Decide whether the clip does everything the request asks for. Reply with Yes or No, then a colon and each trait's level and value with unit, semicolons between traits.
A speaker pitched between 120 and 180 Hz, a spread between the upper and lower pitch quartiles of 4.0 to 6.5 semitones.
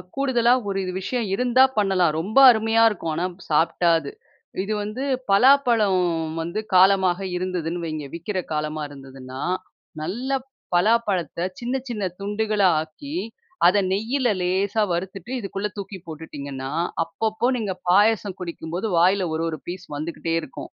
No: high, 190 Hz; average, 4.7 semitones